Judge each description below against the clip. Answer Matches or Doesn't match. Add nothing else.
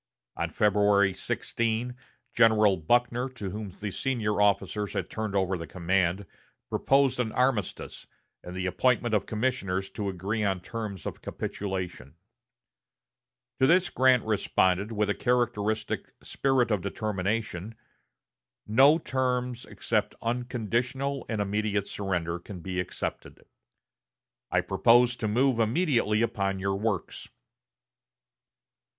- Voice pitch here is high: Doesn't match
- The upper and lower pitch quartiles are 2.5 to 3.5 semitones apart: Doesn't match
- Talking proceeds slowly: Matches